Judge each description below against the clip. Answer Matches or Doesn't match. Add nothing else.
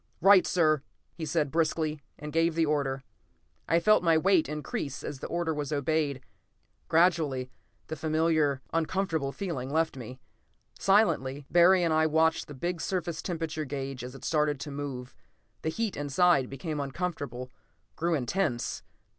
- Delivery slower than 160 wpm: Matches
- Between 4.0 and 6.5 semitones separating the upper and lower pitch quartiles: Doesn't match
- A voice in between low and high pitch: Matches